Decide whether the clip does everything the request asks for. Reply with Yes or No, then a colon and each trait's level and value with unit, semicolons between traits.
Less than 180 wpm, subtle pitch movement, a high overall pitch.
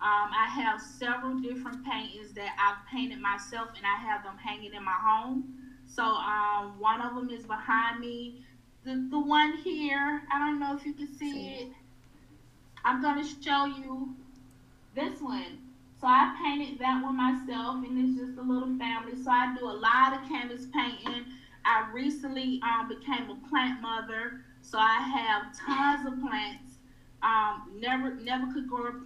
No: average, 170 wpm; average, 3.5 semitones; very high, 255 Hz